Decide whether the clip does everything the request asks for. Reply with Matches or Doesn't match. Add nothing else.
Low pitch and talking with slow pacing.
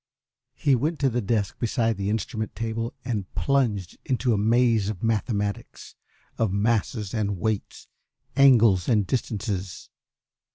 Matches